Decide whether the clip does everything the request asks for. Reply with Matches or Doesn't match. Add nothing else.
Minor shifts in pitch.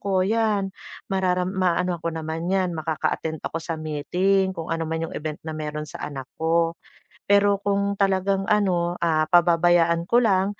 Doesn't match